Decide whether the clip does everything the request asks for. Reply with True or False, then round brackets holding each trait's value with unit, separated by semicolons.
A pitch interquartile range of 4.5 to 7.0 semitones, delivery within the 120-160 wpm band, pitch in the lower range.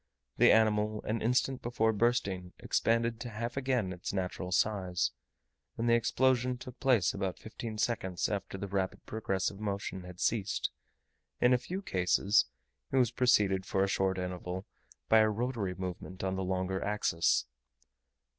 False (3.8 semitones; 155 wpm; 105 Hz)